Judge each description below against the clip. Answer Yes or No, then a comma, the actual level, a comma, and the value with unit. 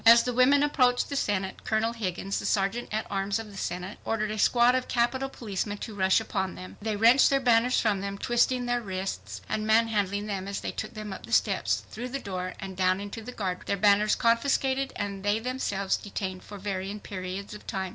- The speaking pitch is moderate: No, high, 210 Hz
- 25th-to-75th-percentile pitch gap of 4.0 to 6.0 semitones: No, average, 3.5 semitones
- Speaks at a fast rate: Yes, fast, 210 wpm